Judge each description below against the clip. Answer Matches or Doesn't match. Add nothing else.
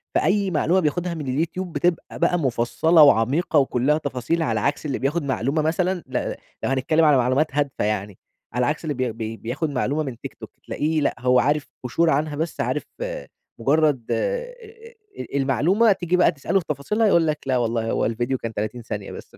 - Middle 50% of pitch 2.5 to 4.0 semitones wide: Doesn't match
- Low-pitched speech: Doesn't match